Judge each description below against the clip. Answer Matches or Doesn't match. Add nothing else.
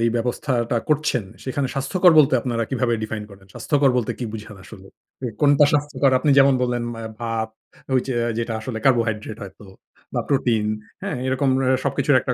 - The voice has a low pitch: Matches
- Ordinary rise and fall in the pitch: Matches